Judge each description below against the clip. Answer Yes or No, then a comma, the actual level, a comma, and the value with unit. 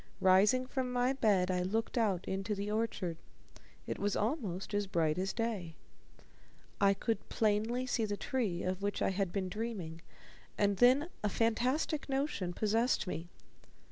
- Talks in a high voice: Yes, high, 205 Hz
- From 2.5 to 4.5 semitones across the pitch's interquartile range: Yes, average, 4.0 semitones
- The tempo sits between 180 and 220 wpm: No, average, 155 wpm